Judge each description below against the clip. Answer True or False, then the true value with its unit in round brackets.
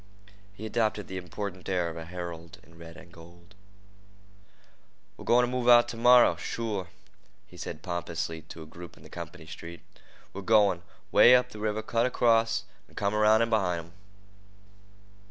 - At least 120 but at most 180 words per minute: True (160 wpm)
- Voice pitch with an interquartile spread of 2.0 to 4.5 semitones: False (4.9 semitones)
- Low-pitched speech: True (100 Hz)